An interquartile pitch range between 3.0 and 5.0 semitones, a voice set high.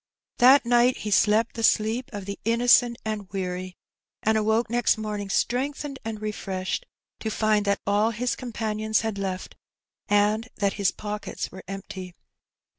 No: narrow, 2.6 semitones; high, 215 Hz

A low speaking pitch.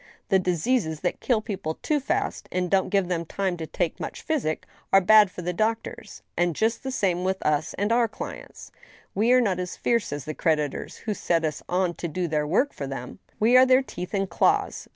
No: medium, 185 Hz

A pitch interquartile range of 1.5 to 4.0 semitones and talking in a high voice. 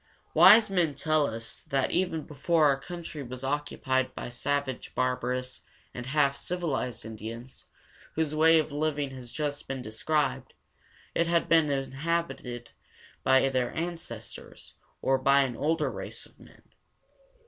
No: average, 3.6 semitones; medium, 140 Hz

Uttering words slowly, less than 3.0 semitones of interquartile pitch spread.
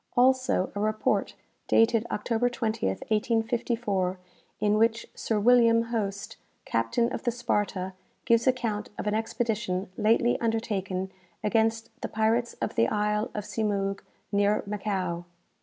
Yes: slow, 125 wpm; narrow, 2.4 semitones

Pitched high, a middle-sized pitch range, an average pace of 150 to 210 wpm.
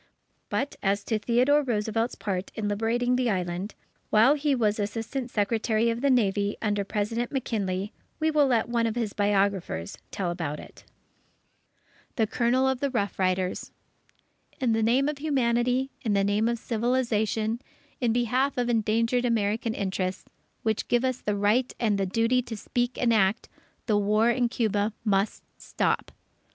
Yes: high, 225 Hz; average, 3.1 semitones; average, 160 wpm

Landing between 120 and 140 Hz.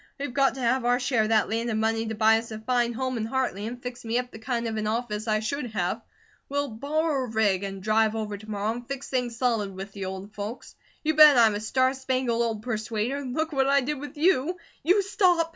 No: high, 235 Hz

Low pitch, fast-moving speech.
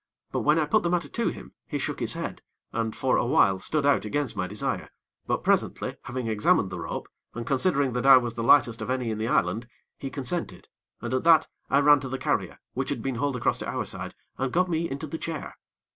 Yes: low, 130 Hz; fast, 235 wpm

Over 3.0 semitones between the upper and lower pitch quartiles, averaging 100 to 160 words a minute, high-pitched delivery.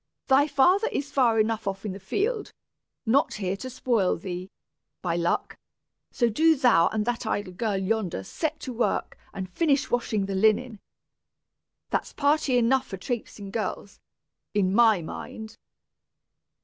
Yes: average, 5.3 semitones; average, 150 wpm; high, 225 Hz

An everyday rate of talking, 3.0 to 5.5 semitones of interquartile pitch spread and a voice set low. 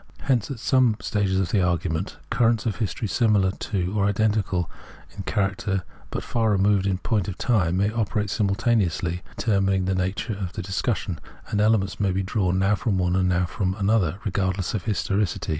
No: average, 190 wpm; narrow, 2.5 semitones; low, 100 Hz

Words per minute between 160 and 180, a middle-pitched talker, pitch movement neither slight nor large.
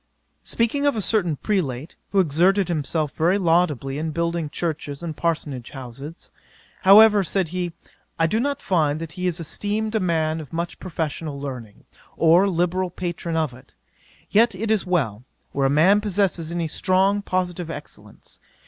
Yes: average, 165 wpm; medium, 170 Hz; average, 3.9 semitones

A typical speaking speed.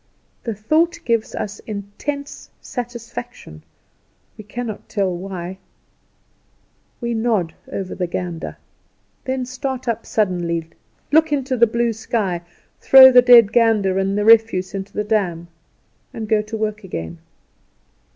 No: slow, 130 wpm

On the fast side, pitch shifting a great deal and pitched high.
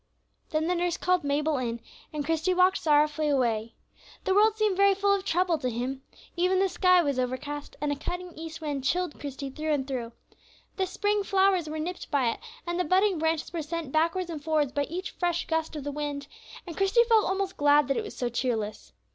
No: fast, 215 wpm; average, 4.3 semitones; very high, 320 Hz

